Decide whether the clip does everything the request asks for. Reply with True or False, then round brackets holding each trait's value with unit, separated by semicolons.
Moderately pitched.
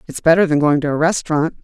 True (155 Hz)